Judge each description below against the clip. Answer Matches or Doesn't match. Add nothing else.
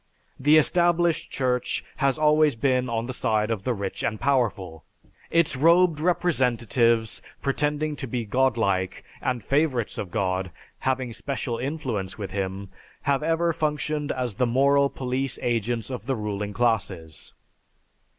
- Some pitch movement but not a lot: Matches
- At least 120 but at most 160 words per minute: Matches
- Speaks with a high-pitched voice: Doesn't match